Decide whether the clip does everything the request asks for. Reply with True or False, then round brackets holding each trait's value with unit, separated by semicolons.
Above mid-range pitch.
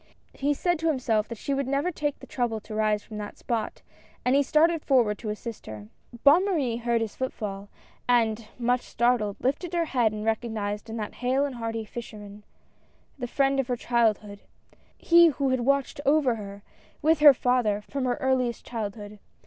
True (240 Hz)